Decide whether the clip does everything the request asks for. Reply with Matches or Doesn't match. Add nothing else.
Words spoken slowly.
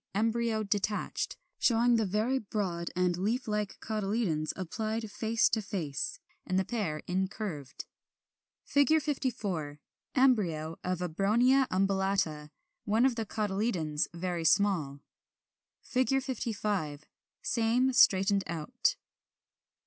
Matches